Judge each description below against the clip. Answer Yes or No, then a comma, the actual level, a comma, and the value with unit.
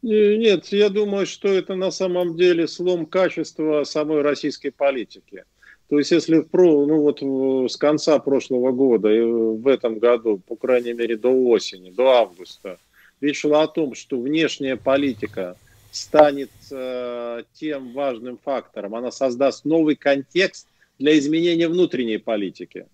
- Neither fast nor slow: Yes, average, 140 wpm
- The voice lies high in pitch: No, medium, 140 Hz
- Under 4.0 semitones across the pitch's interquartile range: No, average, 4.6 semitones